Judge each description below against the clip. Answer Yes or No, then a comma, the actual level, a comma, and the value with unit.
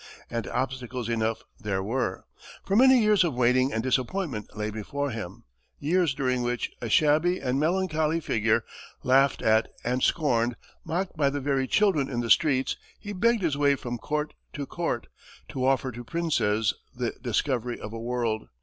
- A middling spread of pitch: Yes, average, 4.8 semitones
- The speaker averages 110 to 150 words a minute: No, average, 170 wpm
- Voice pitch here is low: Yes, low, 130 Hz